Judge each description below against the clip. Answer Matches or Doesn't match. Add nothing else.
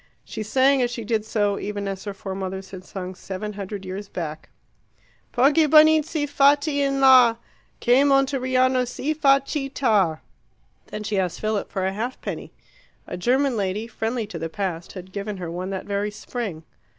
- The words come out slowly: Doesn't match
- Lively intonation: Matches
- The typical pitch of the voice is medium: Doesn't match